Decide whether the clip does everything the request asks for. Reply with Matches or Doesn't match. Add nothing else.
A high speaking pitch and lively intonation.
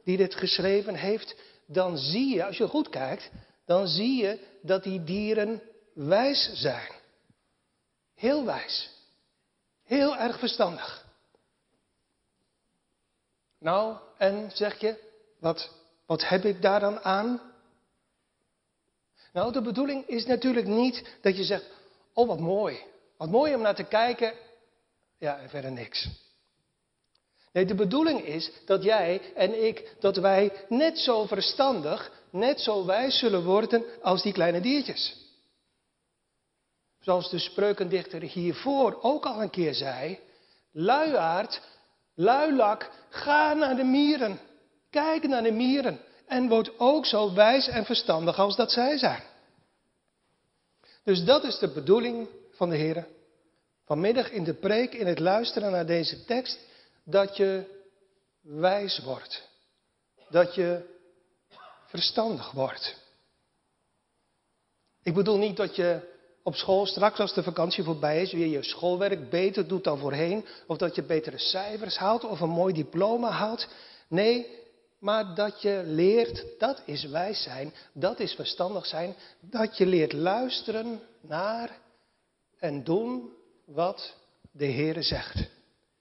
Doesn't match